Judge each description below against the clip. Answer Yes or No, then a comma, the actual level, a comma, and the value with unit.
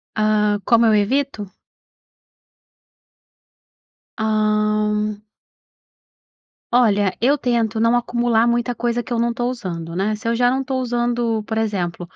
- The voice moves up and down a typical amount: No, narrow, 2.3 semitones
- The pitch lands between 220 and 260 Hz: Yes, high, 225 Hz